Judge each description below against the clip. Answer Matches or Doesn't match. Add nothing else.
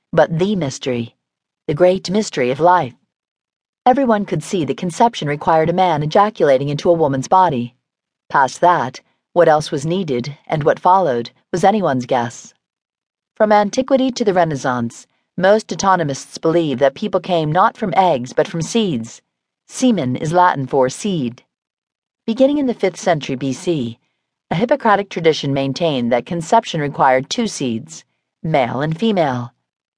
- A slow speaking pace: Doesn't match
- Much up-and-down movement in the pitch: Matches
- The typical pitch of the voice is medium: Matches